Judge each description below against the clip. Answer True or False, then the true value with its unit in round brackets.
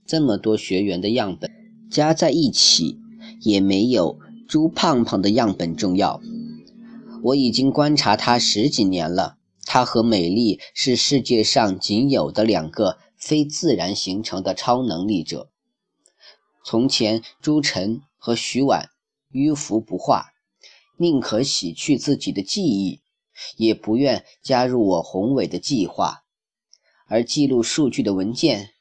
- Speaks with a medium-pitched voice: False (125 Hz)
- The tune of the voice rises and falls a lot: True (6.1 semitones)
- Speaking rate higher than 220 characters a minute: False (200 characters per minute)